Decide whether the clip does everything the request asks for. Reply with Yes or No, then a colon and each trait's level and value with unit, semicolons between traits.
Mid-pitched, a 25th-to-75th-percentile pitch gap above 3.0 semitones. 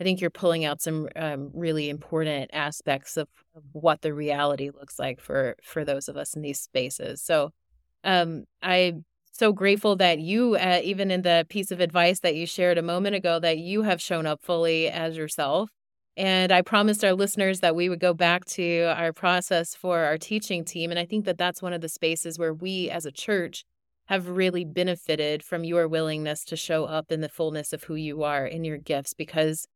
No: medium, 170 Hz; narrow, 2.6 semitones